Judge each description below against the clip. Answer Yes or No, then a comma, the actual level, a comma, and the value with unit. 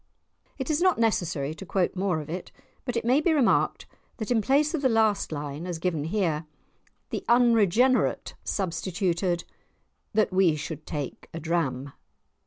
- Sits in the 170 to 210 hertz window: Yes, medium, 185 Hz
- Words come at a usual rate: Yes, average, 160 wpm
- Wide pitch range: Yes, wide, 6.5 semitones